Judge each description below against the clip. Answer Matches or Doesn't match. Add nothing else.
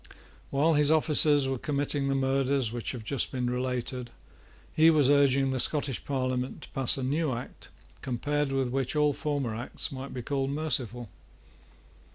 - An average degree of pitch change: Doesn't match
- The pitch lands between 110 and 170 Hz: Matches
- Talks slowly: Doesn't match